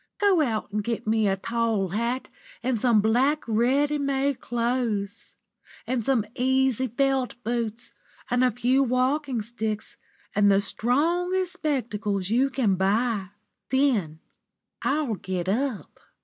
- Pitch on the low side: No, high, 240 Hz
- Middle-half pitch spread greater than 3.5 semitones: Yes, average, 4.0 semitones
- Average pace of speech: No, slow, 130 wpm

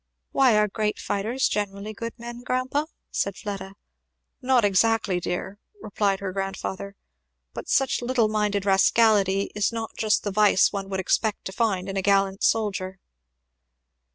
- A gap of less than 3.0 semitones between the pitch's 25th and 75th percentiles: Yes, narrow, 2.6 semitones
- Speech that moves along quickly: No, average, 150 wpm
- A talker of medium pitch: No, high, 205 Hz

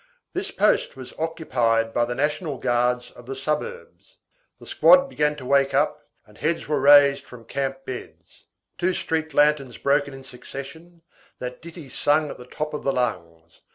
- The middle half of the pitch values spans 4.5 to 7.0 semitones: No, average, 3.7 semitones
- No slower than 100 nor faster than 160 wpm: No, average, 170 wpm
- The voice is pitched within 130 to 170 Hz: Yes, medium, 140 Hz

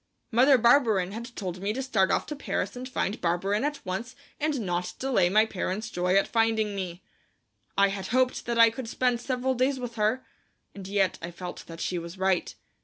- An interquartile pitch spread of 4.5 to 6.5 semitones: Yes, average, 4.9 semitones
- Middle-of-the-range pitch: No, high, 215 Hz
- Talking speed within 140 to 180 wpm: No, average, 200 wpm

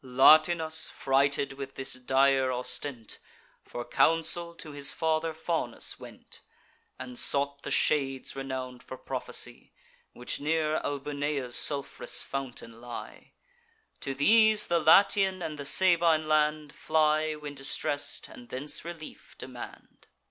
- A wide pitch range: No, average, 2.9 semitones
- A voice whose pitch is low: No, medium, 145 Hz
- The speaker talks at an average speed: No, slow, 120 wpm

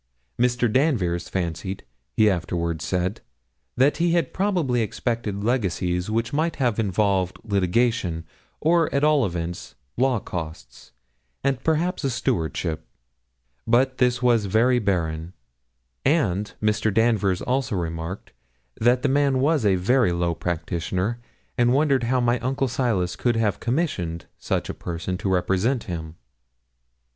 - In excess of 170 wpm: No, slow, 135 wpm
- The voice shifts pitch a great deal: Yes, wide, 6.3 semitones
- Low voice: Yes, low, 110 Hz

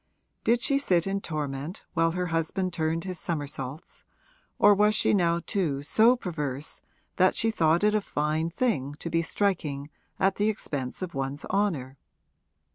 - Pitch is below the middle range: No, medium, 170 Hz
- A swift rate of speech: No, average, 160 wpm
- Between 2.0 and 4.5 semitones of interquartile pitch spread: No, average, 5.0 semitones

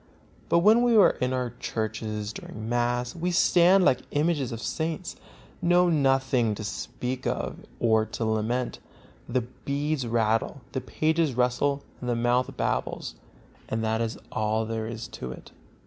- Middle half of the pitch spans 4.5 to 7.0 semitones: Yes, average, 4.8 semitones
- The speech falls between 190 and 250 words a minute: No, average, 155 wpm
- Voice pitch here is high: No, low, 125 Hz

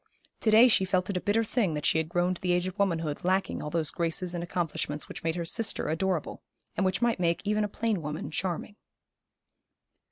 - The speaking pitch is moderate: Yes, medium, 180 Hz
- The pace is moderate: No, fast, 220 wpm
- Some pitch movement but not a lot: Yes, average, 3.5 semitones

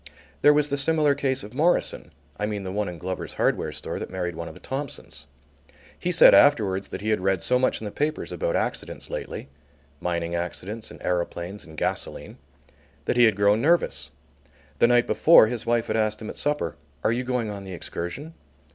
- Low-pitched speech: Yes, low, 110 Hz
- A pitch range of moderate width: No, wide, 6.3 semitones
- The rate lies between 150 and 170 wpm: No, average, 200 wpm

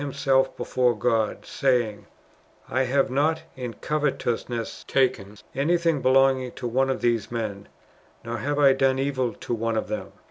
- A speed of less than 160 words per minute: Yes, average, 150 wpm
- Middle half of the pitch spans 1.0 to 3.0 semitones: Yes, average, 2.7 semitones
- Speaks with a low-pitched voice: Yes, low, 130 Hz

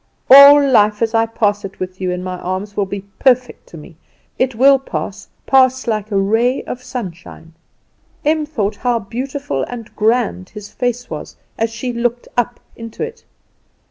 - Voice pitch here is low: No, high, 225 Hz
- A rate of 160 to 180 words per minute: Yes, average, 170 wpm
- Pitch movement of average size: Yes, average, 4.0 semitones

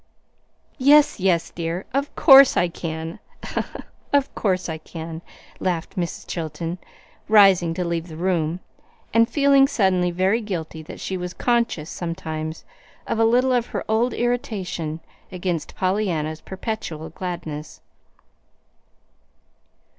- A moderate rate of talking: No, slow, 120 wpm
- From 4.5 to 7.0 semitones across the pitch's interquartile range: Yes, average, 5.2 semitones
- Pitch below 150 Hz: No, medium, 180 Hz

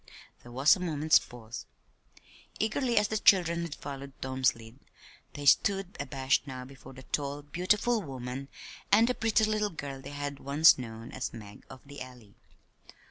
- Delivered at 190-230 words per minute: No, average, 165 wpm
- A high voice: No, medium, 140 Hz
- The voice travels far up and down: Yes, wide, 5.8 semitones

